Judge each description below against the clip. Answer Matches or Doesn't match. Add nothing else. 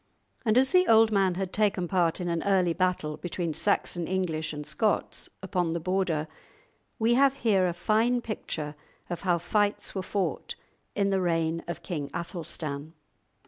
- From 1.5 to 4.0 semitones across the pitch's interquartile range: Matches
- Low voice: Doesn't match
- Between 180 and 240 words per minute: Doesn't match